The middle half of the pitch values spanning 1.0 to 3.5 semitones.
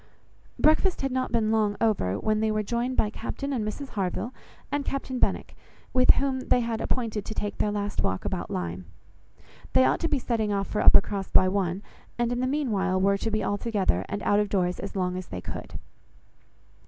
No: average, 4.1 semitones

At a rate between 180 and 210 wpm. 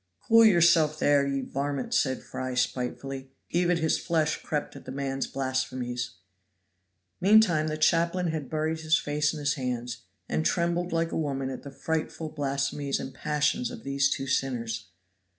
No: average, 160 wpm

